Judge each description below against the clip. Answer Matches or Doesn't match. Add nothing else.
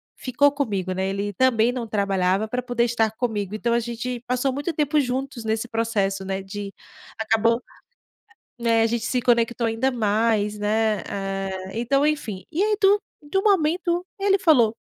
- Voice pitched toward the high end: Matches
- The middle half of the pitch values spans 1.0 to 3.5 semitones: Doesn't match